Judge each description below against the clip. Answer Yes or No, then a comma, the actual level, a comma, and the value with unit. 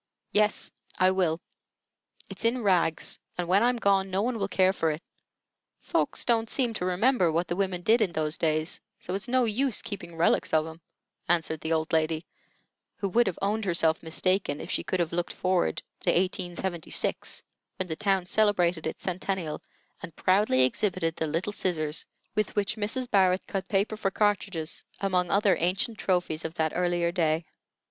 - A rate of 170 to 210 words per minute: Yes, average, 175 wpm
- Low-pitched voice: No, medium, 185 Hz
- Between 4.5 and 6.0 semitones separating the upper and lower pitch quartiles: No, average, 3.8 semitones